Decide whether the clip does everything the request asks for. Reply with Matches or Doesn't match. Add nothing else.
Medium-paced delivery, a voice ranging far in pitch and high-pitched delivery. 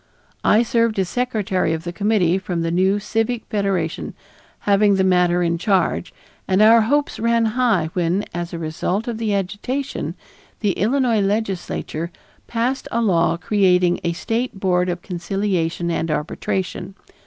Doesn't match